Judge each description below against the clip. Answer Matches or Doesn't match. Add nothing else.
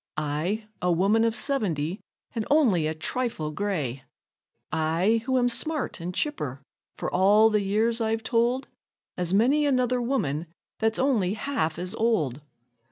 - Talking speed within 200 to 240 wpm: Doesn't match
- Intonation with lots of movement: Matches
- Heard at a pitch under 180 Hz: Doesn't match